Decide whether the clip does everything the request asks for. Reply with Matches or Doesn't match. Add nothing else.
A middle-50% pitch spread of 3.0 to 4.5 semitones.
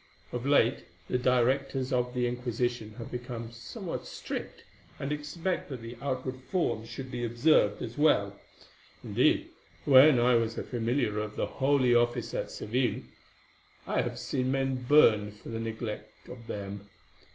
Doesn't match